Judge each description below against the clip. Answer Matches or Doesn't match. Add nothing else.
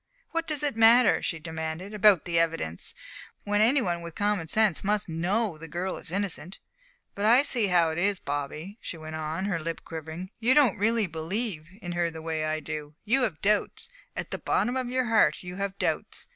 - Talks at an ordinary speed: Doesn't match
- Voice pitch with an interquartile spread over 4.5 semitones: Matches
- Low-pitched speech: Doesn't match